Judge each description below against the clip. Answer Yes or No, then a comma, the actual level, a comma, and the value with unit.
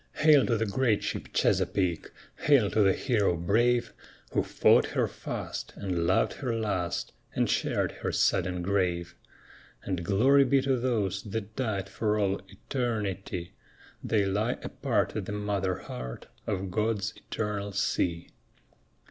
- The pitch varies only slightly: No, average, 3.3 semitones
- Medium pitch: No, low, 100 Hz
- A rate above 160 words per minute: No, average, 140 wpm